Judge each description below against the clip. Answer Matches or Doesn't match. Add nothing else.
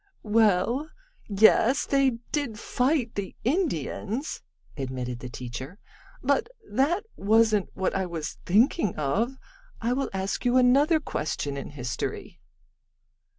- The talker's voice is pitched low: Doesn't match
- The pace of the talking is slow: Matches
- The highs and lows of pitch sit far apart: Matches